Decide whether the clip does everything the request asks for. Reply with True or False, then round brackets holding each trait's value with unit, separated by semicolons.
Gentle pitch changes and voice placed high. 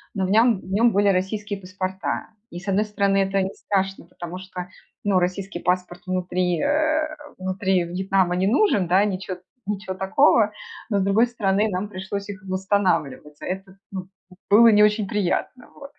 True (2.1 semitones; 195 Hz)